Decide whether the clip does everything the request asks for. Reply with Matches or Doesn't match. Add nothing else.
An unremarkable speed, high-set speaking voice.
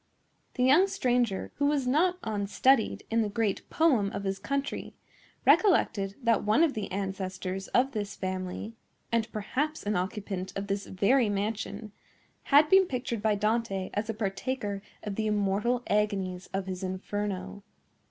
Matches